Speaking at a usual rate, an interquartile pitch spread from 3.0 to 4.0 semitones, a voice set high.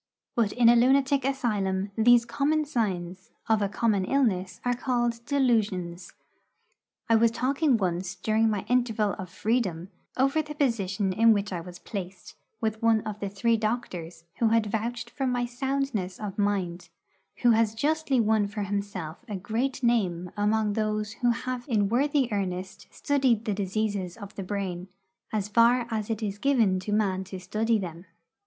Yes: average, 165 wpm; average, 3.7 semitones; high, 215 Hz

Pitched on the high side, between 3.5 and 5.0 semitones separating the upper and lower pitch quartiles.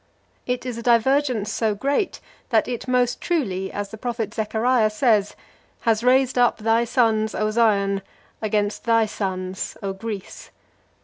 No: high, 225 Hz; average, 2.9 semitones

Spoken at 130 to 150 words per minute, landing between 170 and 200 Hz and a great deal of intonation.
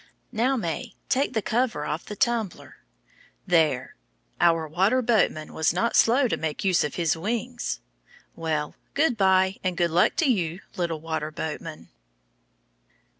Yes: average, 145 wpm; medium, 185 Hz; wide, 6.3 semitones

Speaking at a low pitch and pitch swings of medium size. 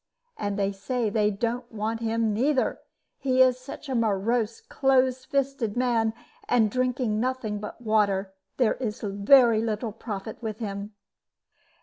No: high, 225 Hz; average, 3.2 semitones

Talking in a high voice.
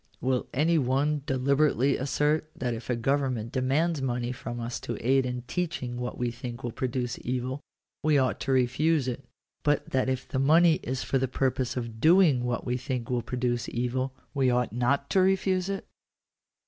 No: low, 130 Hz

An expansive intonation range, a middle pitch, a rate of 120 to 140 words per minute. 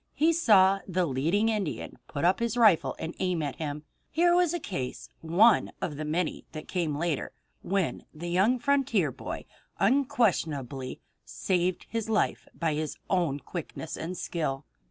No: wide, 6.2 semitones; medium, 180 Hz; average, 160 wpm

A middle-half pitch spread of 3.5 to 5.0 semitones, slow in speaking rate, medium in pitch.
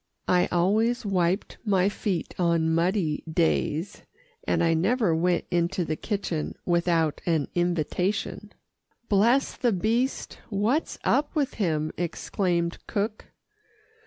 Yes: average, 3.8 semitones; slow, 115 wpm; medium, 180 Hz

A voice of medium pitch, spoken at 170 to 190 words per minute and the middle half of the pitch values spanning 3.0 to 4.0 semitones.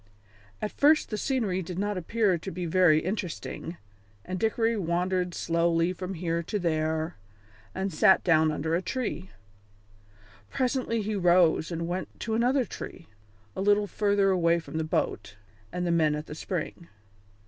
No: medium, 180 Hz; average, 160 wpm; average, 3.7 semitones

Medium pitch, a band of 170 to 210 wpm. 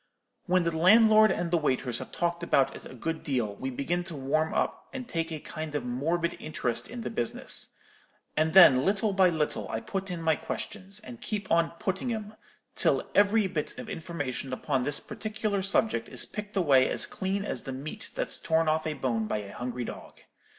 Yes: medium, 165 Hz; average, 200 wpm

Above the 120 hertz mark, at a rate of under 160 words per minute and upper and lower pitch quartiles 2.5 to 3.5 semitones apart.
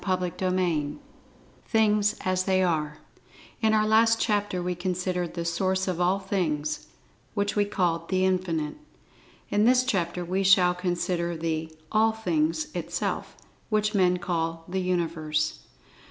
Yes: medium, 185 Hz; average, 145 wpm; average, 3.1 semitones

